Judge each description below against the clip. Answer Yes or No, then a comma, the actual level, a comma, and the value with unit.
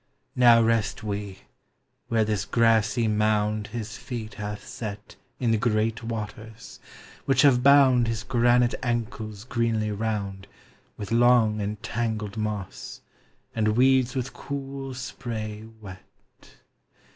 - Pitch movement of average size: No, narrow, 2.3 semitones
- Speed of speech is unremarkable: No, slow, 120 wpm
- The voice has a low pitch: Yes, low, 110 Hz